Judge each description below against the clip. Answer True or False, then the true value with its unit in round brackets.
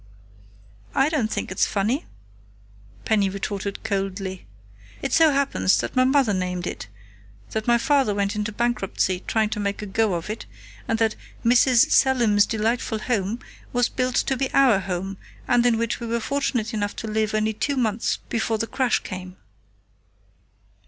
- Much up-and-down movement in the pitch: False (3.4 semitones)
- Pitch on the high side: True (220 Hz)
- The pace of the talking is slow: False (165 wpm)